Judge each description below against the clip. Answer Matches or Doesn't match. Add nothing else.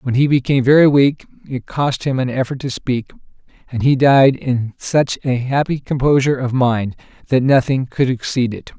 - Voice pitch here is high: Doesn't match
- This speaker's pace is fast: Doesn't match